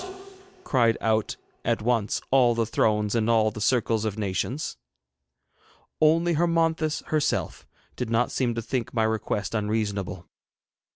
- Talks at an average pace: No, slow, 130 wpm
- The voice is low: Yes, low, 115 Hz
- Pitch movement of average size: Yes, average, 3.3 semitones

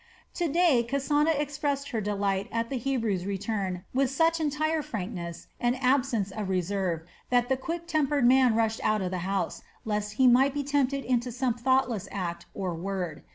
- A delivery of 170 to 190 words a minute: Yes, average, 175 wpm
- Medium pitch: No, high, 240 Hz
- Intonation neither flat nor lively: No, wide, 5.8 semitones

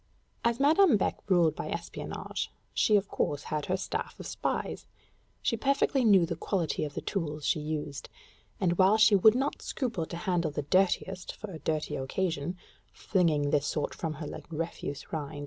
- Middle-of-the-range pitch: Yes, medium, 175 Hz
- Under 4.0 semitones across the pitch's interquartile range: No, average, 5.0 semitones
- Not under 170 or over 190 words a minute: Yes, average, 180 wpm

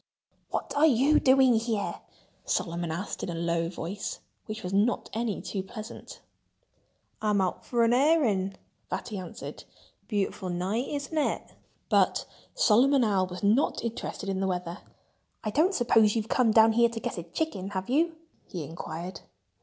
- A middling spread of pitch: Yes, average, 4.5 semitones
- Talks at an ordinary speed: Yes, average, 160 wpm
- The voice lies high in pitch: Yes, high, 215 Hz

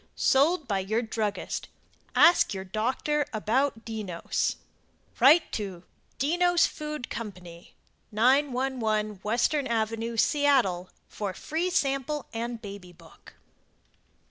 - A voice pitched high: Yes, high, 235 Hz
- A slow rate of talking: Yes, slow, 100 wpm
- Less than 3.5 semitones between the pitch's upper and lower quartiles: No, average, 5.2 semitones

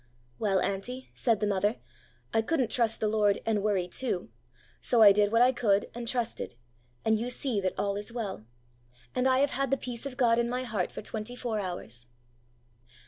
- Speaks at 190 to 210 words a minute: Yes, average, 195 wpm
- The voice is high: Yes, high, 225 Hz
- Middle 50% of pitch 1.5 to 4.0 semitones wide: Yes, average, 3.4 semitones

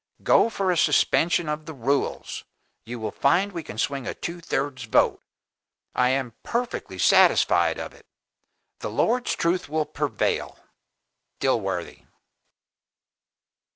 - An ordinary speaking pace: No, slow, 125 wpm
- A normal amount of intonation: No, wide, 5.8 semitones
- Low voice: No, medium, 150 Hz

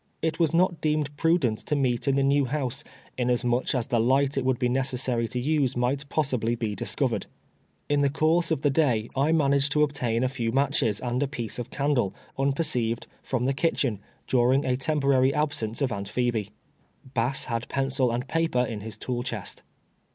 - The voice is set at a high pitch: No, low, 130 Hz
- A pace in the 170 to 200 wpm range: Yes, average, 190 wpm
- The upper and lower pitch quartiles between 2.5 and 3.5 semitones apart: Yes, average, 3.0 semitones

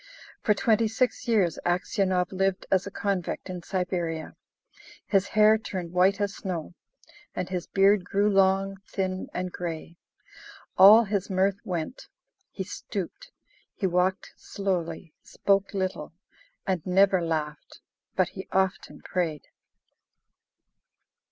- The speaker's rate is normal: No, slow, 120 wpm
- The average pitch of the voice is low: No, high, 190 Hz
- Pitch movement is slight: Yes, narrow, 1.9 semitones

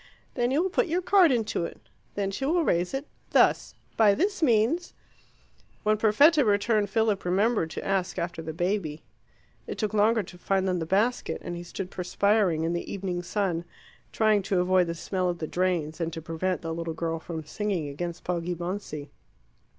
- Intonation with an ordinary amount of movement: Yes, average, 4.2 semitones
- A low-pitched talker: No, high, 190 Hz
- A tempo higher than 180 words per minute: Yes, average, 190 wpm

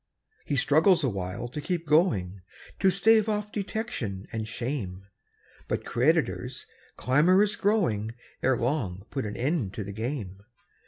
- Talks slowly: Yes, slow, 130 wpm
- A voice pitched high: No, low, 130 Hz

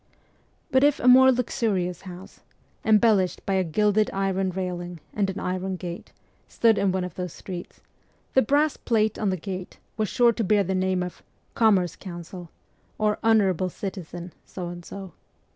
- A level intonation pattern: No, average, 3.0 semitones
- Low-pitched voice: No, high, 190 Hz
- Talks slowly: No, average, 180 wpm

